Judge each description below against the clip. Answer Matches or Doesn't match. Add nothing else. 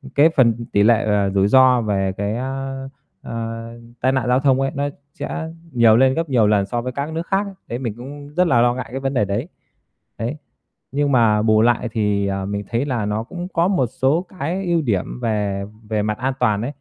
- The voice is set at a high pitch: Doesn't match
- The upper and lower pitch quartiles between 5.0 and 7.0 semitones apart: Doesn't match